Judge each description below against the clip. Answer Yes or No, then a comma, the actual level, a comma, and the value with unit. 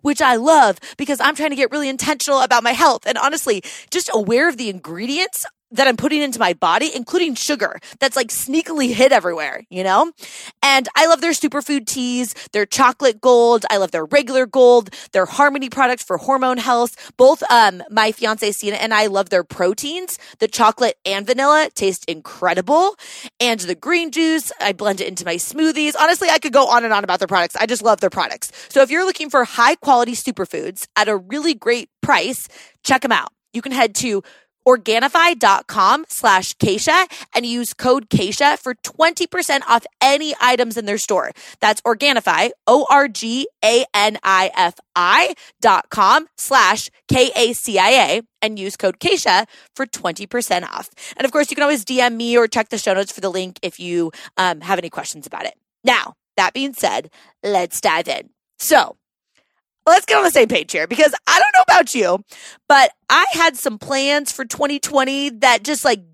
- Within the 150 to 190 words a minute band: Yes, average, 180 wpm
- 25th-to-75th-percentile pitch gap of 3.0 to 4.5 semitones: No, wide, 5.5 semitones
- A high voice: Yes, very high, 255 Hz